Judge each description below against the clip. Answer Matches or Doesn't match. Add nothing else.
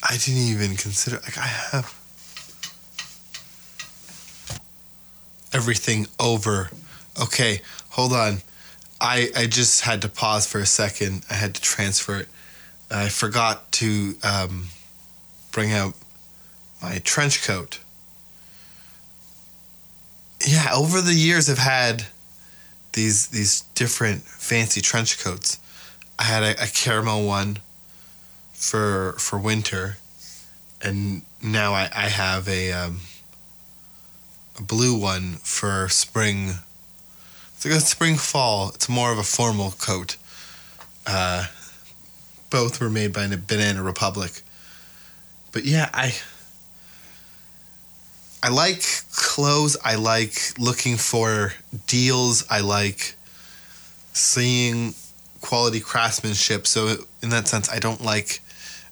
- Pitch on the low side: Matches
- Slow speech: Matches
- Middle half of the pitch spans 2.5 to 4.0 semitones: Matches